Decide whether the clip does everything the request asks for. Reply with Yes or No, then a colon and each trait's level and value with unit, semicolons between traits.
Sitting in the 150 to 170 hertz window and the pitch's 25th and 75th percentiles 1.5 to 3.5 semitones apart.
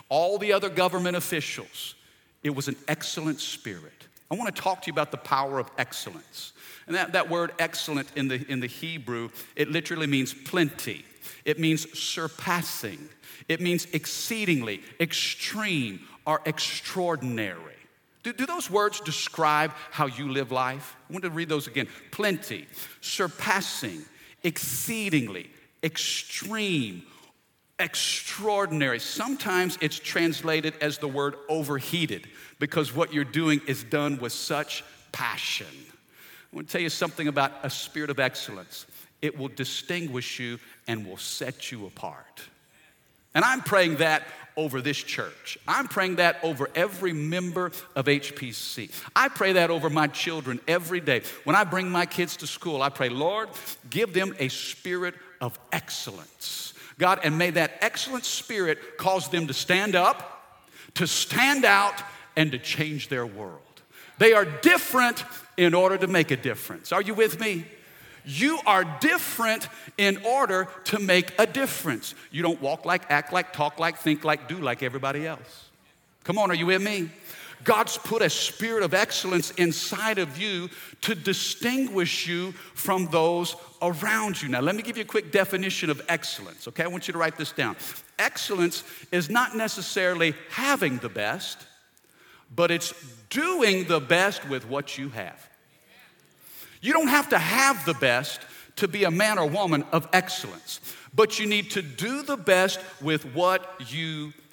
No: medium, 165 Hz; average, 4.5 semitones